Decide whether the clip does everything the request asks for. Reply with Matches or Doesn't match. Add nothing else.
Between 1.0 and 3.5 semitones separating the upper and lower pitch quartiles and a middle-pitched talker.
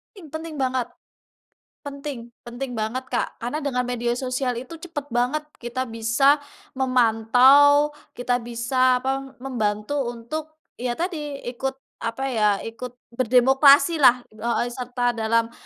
Doesn't match